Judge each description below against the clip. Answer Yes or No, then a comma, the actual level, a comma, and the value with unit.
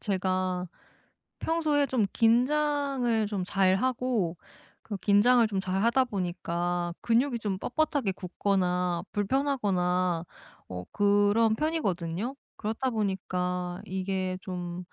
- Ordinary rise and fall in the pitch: Yes, average, 5.0 semitones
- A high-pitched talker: Yes, high, 200 Hz